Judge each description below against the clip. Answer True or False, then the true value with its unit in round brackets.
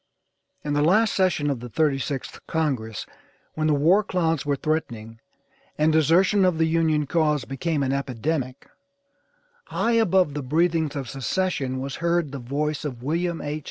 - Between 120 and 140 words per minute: False (160 wpm)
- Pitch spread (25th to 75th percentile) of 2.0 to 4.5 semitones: True (3.5 semitones)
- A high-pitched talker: False (150 Hz)